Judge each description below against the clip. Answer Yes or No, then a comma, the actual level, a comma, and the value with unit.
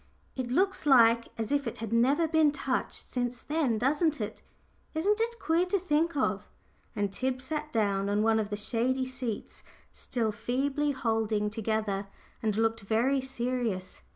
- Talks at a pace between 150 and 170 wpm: Yes, average, 160 wpm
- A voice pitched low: No, high, 245 Hz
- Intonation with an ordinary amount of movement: Yes, average, 4.8 semitones